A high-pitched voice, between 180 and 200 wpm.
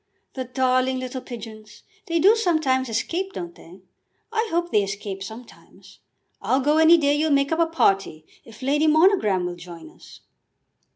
No: very high, 260 Hz; average, 165 wpm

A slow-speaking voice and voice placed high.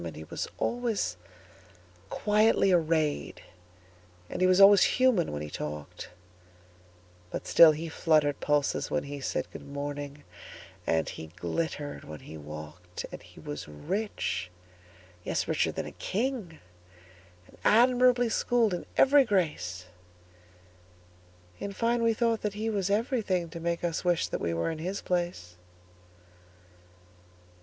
No: slow, 120 wpm; medium, 140 Hz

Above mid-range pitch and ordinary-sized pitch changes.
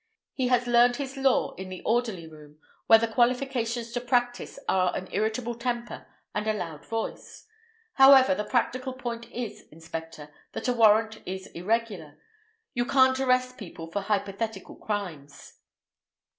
Yes: high, 225 Hz; average, 4.5 semitones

